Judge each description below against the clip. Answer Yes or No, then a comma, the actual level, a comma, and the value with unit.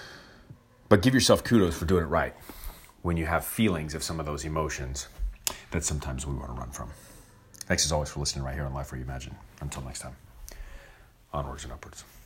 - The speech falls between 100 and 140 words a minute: No, fast, 205 wpm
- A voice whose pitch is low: Yes, very low, 75 Hz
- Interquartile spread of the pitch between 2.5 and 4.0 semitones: No, average, 4.8 semitones